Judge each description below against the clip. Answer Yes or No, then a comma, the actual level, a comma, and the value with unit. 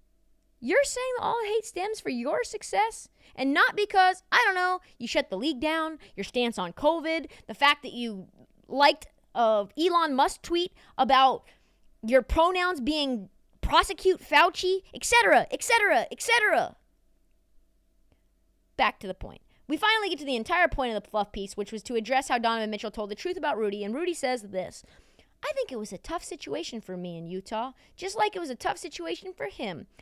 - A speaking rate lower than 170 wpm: No, average, 180 wpm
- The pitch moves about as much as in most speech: No, wide, 8.2 semitones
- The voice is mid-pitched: No, very high, 295 Hz